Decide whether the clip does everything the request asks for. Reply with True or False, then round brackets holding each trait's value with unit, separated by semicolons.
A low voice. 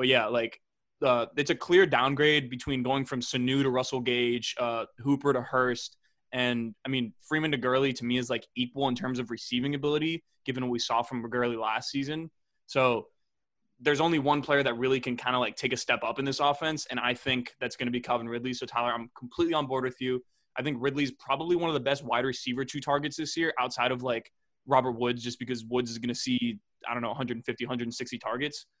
True (130 Hz)